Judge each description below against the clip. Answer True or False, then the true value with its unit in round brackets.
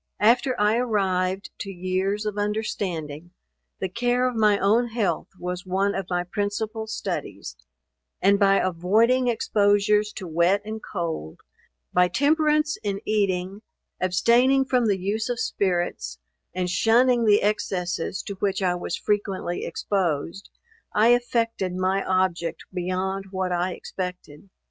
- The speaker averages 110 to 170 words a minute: True (135 wpm)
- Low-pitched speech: False (195 Hz)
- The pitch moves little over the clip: False (3.3 semitones)